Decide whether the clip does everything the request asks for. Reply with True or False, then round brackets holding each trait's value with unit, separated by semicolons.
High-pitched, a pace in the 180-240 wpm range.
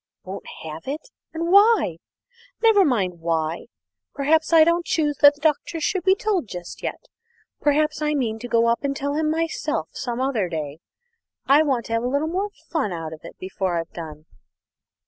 True (275 Hz; 185 wpm)